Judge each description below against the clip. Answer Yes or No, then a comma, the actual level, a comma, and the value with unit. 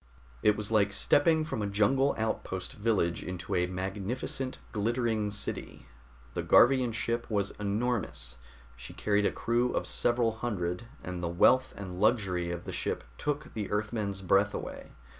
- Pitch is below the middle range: Yes, low, 105 Hz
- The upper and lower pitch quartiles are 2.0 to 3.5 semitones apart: No, average, 3.9 semitones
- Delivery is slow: No, average, 155 wpm